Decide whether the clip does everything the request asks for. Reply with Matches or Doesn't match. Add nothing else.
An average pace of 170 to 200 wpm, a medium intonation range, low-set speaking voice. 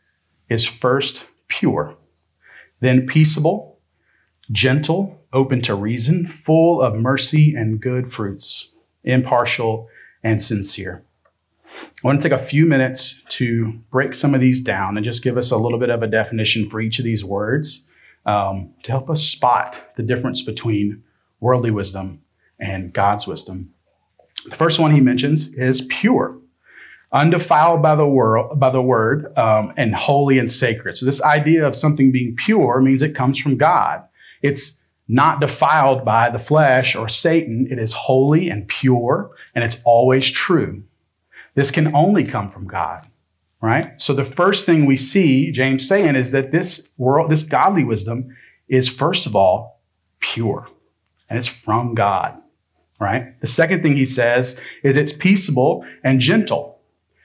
Doesn't match